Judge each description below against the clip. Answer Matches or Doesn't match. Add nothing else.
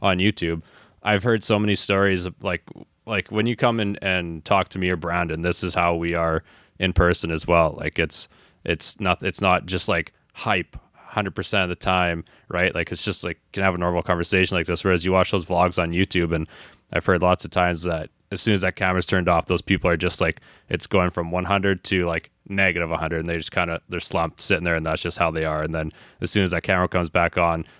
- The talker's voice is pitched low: Matches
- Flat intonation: Matches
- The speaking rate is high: Matches